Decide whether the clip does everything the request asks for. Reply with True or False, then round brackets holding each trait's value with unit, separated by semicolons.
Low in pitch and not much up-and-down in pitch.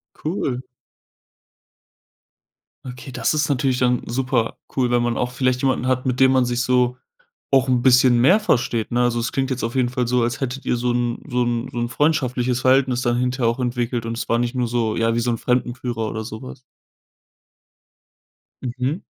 True (125 Hz; 1.3 semitones)